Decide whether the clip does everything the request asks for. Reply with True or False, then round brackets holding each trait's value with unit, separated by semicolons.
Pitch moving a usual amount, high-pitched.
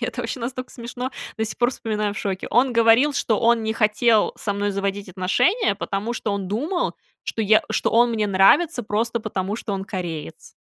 True (3.1 semitones; 220 Hz)